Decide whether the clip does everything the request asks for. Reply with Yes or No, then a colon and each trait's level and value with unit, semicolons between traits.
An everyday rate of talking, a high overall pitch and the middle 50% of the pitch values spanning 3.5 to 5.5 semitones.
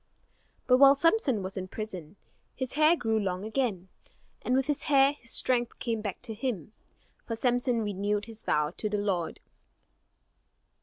Yes: average, 160 wpm; high, 225 Hz; average, 4.3 semitones